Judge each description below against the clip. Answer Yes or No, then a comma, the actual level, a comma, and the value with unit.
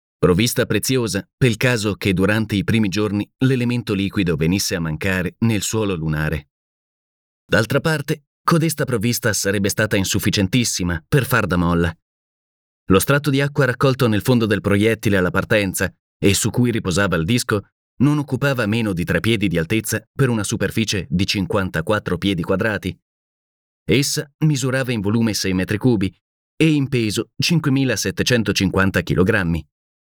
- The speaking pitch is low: Yes, low, 105 Hz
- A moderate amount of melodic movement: Yes, average, 4.4 semitones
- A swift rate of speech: No, average, 145 wpm